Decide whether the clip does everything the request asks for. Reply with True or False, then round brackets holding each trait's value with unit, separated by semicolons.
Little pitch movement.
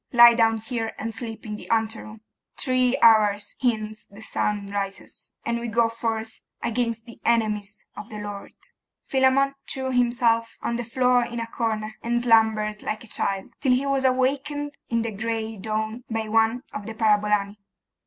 True (1.9 semitones)